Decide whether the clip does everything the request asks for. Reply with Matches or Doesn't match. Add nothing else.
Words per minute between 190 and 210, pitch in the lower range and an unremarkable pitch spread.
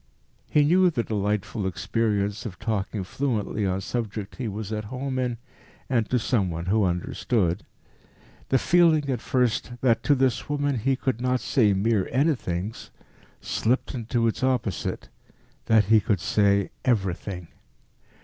Doesn't match